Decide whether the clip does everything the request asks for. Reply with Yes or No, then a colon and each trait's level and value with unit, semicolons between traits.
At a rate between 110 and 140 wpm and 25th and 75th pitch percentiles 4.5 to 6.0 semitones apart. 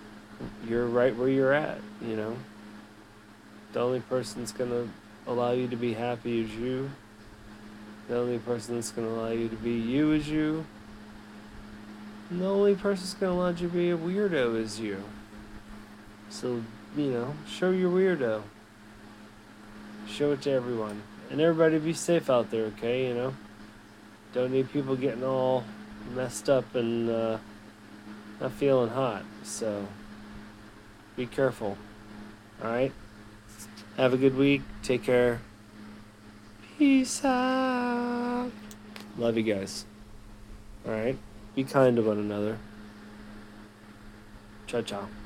No: slow, 135 wpm; average, 3.6 semitones